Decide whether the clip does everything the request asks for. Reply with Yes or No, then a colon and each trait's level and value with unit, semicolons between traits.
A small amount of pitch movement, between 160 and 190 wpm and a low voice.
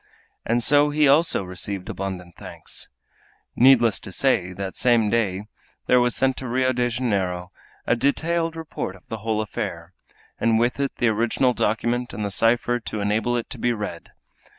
No: average, 3.8 semitones; average, 175 wpm; low, 115 Hz